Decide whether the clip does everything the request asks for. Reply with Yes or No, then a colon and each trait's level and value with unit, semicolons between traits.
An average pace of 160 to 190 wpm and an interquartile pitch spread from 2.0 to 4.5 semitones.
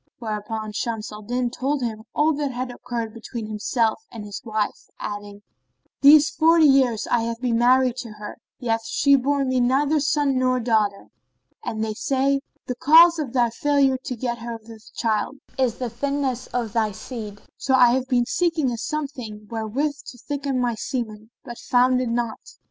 Yes: average, 180 wpm; average, 3.5 semitones